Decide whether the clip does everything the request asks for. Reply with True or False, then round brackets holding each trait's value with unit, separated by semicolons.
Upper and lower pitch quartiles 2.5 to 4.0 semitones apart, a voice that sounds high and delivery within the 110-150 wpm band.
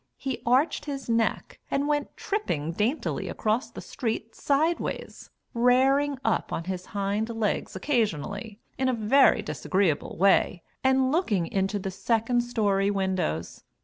False (5.1 semitones; 225 Hz; 135 wpm)